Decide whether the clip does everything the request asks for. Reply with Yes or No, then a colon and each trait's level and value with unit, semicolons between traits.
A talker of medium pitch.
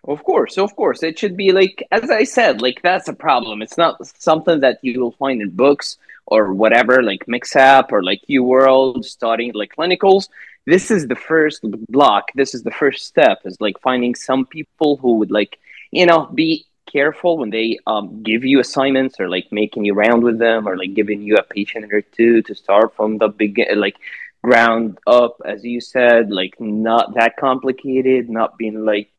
No: low, 125 Hz